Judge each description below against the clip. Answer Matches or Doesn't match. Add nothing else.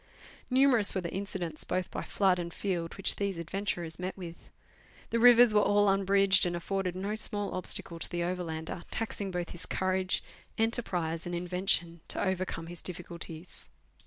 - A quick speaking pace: Doesn't match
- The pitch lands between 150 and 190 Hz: Matches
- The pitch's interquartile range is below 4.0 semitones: Matches